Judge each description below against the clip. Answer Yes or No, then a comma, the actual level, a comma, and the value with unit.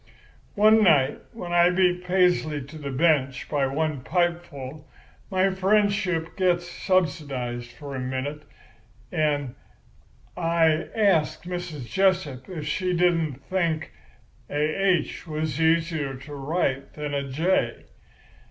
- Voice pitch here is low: No, medium, 160 Hz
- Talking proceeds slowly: Yes, slow, 120 wpm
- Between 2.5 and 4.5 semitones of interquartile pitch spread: Yes, average, 4.1 semitones